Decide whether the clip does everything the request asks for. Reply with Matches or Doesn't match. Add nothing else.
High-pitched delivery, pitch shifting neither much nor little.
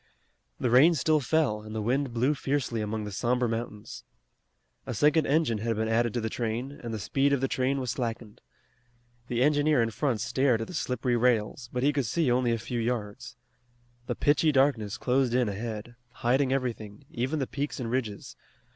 Doesn't match